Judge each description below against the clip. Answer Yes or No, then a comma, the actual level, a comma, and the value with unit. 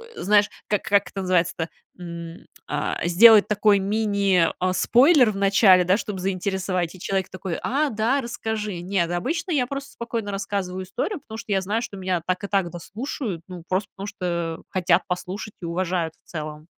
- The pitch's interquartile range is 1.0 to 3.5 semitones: Yes, average, 3.0 semitones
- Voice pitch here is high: Yes, high, 195 Hz